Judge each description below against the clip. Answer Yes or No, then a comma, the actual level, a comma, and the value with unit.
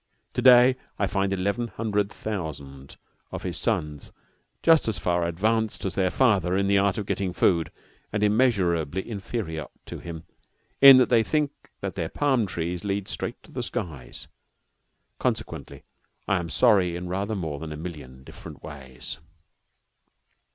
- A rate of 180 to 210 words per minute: No, average, 155 wpm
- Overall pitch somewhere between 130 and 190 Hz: No, very low, 95 Hz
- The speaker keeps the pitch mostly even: No, average, 4.7 semitones